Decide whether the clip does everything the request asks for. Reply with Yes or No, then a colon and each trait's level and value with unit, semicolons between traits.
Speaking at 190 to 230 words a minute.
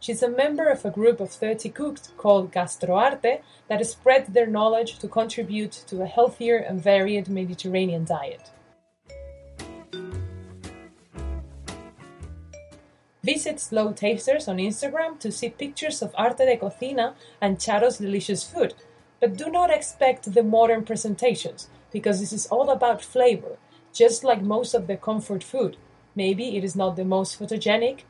No: average, 145 wpm